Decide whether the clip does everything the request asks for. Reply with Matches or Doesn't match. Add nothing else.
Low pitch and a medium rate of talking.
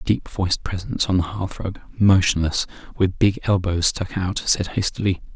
Matches